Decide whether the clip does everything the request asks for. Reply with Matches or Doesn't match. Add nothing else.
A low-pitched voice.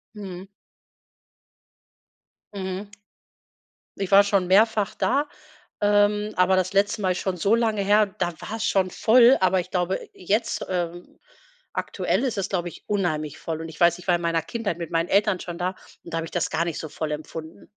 Doesn't match